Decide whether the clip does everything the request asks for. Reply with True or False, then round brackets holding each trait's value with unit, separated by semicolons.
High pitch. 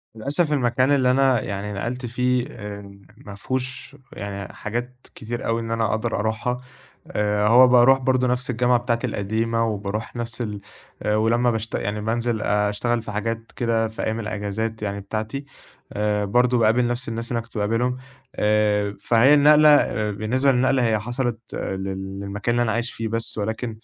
False (115 Hz)